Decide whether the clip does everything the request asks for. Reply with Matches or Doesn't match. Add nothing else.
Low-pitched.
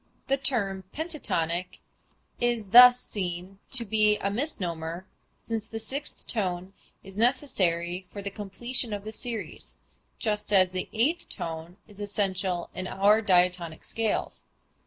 Doesn't match